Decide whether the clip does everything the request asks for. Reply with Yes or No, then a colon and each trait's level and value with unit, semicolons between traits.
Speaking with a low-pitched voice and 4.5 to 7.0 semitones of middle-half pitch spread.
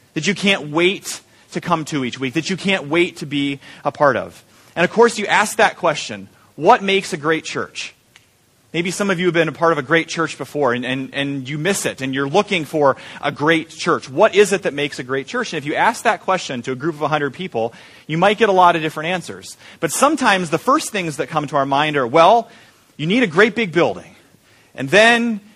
No: medium, 165 Hz; wide, 5.6 semitones